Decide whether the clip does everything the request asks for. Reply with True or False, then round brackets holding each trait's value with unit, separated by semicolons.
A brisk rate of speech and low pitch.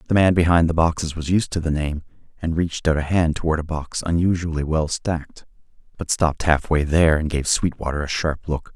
True (210 wpm; 80 Hz)